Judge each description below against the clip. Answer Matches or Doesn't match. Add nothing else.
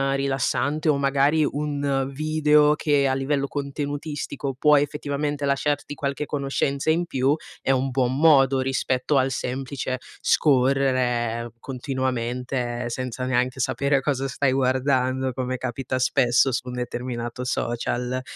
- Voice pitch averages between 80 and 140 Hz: Matches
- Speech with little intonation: Matches